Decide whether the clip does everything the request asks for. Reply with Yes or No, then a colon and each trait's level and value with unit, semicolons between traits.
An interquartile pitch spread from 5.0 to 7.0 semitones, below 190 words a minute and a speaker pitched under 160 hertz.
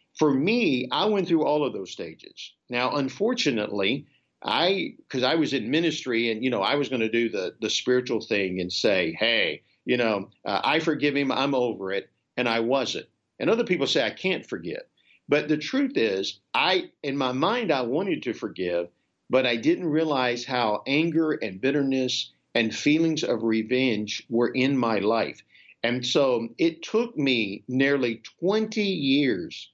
Yes: wide, 5.5 semitones; average, 175 wpm; low, 135 Hz